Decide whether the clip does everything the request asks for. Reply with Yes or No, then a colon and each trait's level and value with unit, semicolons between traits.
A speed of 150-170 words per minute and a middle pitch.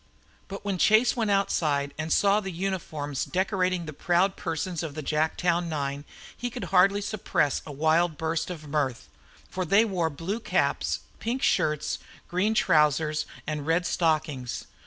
Yes: average, 155 wpm; medium, 170 Hz